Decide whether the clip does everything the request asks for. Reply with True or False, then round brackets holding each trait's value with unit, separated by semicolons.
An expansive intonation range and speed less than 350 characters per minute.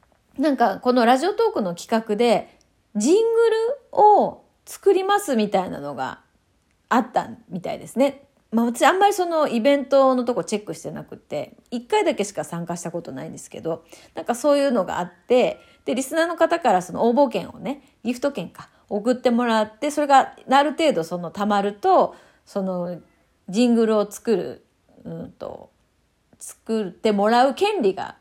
True (6.2 semitones; 340 characters per minute)